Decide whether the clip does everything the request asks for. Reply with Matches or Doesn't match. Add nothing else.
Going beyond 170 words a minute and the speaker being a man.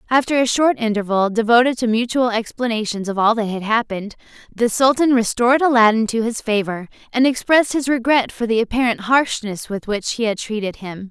Doesn't match